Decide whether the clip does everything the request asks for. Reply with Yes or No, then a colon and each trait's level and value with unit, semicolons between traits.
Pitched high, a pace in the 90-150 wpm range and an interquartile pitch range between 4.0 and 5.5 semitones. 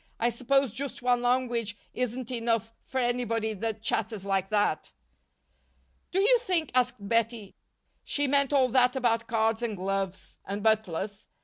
No: high, 230 Hz; average, 145 wpm; average, 2.8 semitones